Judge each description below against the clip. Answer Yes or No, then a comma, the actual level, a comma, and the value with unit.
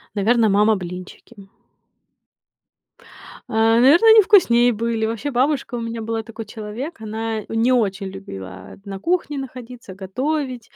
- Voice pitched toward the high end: Yes, high, 225 Hz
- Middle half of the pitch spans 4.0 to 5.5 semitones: No, average, 3.3 semitones